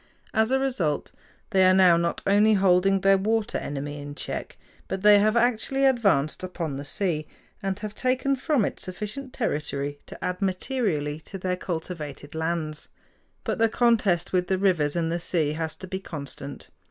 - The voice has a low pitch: No, medium, 185 Hz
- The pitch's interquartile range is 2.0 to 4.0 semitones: No, average, 5.2 semitones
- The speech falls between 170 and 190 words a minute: Yes, average, 175 wpm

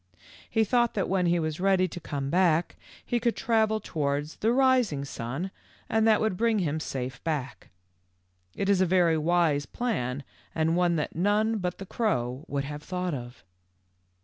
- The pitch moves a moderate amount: No, wide, 6.4 semitones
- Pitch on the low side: No, medium, 175 Hz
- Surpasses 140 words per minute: Yes, average, 180 wpm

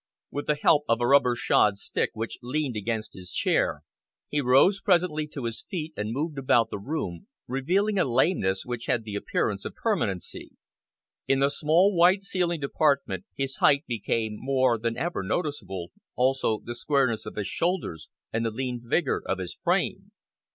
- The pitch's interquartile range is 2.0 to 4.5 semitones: No, wide, 5.5 semitones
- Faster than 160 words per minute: Yes, average, 170 wpm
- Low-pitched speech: Yes, low, 130 Hz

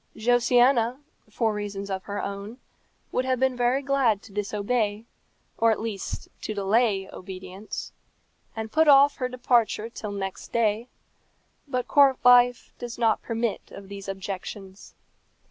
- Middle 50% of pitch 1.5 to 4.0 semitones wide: Yes, average, 3.6 semitones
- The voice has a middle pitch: No, high, 225 Hz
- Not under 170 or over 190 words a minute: No, average, 140 wpm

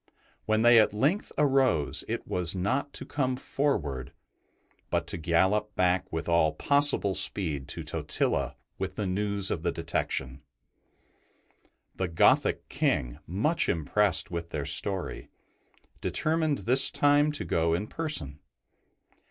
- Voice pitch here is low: Yes, very low, 95 Hz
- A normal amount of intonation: No, wide, 8.4 semitones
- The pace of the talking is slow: Yes, slow, 130 wpm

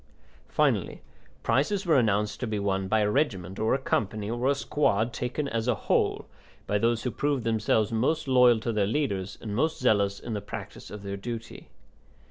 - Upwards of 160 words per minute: Yes, average, 190 wpm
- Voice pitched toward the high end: No, low, 110 Hz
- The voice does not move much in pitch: No, average, 3.7 semitones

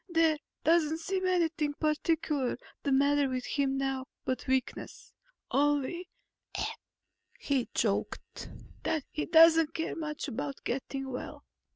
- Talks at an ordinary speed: No, slow, 115 wpm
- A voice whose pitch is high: Yes, very high, 295 Hz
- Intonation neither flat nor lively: Yes, average, 3.3 semitones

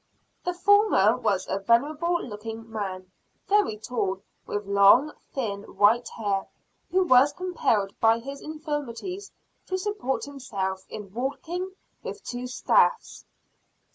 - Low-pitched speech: No, high, 245 Hz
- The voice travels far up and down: Yes, wide, 8.4 semitones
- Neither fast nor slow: No, slow, 120 wpm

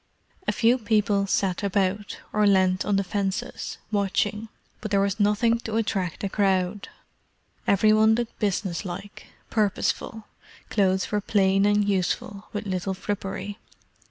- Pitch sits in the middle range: No, high, 200 Hz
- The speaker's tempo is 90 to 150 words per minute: Yes, average, 140 wpm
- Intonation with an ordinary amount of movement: No, narrow, 1.7 semitones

